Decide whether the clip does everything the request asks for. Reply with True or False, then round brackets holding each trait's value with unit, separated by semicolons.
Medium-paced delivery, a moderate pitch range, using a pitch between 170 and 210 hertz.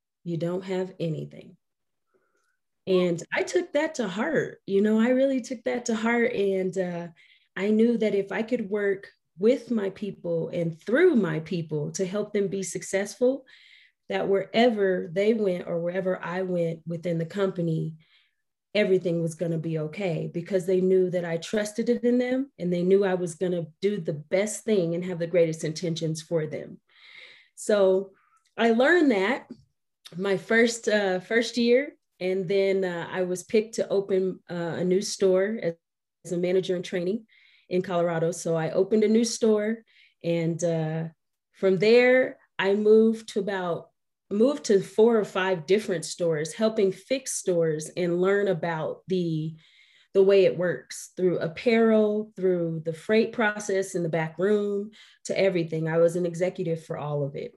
True (170 wpm; 3.9 semitones; 190 Hz)